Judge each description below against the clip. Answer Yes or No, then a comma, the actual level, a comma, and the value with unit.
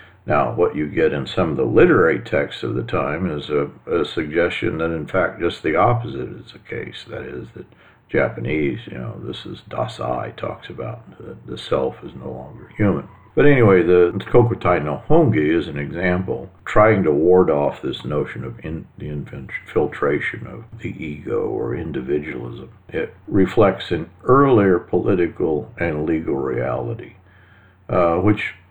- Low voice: Yes, very low, 90 Hz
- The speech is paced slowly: No, average, 165 wpm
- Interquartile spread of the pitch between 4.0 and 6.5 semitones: Yes, average, 4.8 semitones